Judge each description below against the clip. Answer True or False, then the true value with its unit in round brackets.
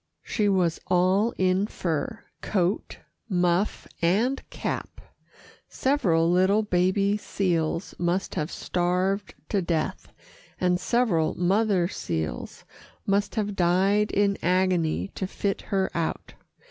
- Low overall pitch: False (185 Hz)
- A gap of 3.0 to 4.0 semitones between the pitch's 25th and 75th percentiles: False (2.6 semitones)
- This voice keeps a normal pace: False (110 wpm)